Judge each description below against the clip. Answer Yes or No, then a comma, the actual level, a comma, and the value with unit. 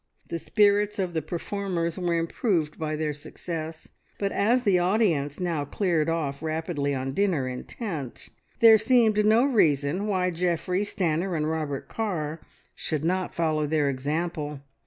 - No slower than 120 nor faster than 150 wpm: Yes, average, 145 wpm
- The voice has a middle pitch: Yes, medium, 165 Hz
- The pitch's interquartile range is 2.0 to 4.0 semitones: No, average, 4.6 semitones